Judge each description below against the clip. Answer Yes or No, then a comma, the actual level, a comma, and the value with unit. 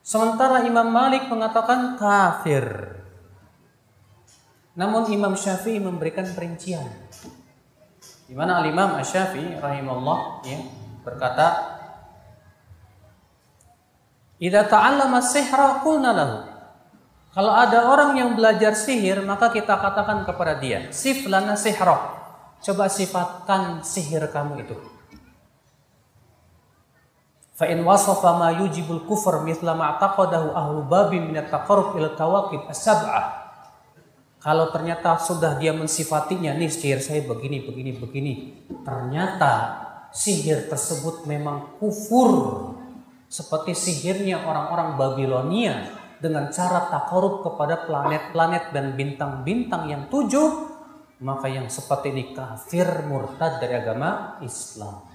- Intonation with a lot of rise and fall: Yes, wide, 6.4 semitones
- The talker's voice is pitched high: No, medium, 165 Hz